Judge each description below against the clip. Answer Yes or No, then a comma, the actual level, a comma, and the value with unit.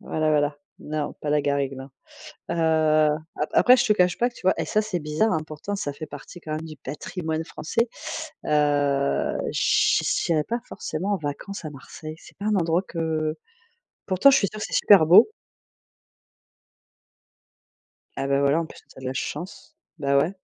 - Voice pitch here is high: No, medium, 155 Hz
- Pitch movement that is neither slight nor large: Yes, average, 4.2 semitones